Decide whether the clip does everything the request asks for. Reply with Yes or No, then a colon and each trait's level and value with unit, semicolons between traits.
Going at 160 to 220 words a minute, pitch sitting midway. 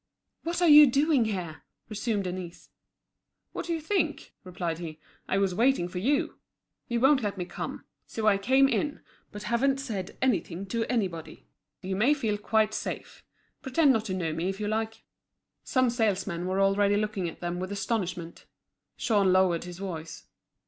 No: average, 170 wpm; high, 205 Hz